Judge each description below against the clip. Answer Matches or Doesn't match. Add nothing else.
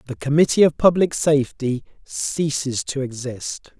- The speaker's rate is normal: Doesn't match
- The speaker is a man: Matches